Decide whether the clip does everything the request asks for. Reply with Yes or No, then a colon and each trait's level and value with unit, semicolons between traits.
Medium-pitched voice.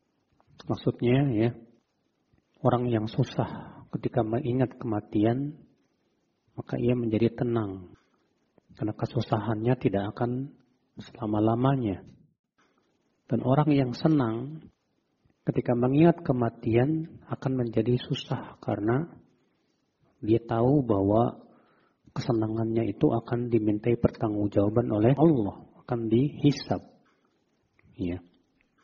No: low, 120 Hz